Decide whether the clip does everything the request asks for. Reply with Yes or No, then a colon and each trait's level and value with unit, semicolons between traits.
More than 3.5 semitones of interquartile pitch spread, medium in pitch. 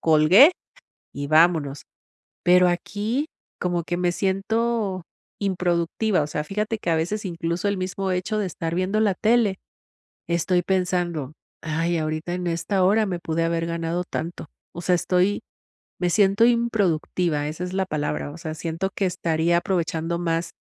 No: average, 2.8 semitones; medium, 175 Hz